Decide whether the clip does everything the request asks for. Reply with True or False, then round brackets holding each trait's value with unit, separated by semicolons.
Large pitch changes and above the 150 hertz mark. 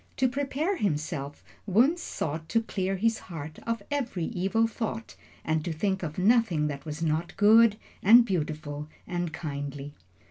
True (6.6 semitones; 185 Hz)